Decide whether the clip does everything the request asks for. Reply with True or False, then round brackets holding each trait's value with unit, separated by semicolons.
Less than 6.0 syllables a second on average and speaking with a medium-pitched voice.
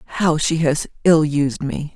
True (4.3 syllables/s; 155 Hz)